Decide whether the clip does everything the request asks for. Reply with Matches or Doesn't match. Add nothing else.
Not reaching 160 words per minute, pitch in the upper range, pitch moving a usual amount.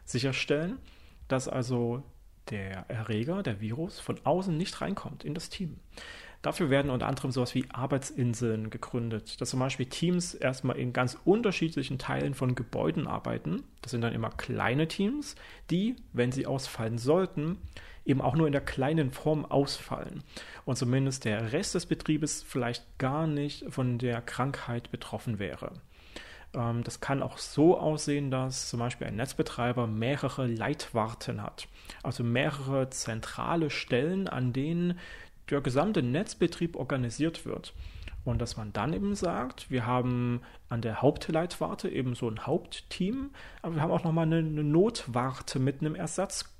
Doesn't match